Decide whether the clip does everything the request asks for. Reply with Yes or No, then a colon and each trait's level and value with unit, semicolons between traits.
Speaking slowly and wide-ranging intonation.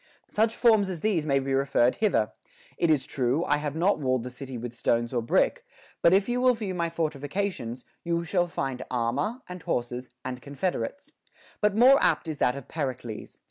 No: average, 195 wpm; wide, 6.9 semitones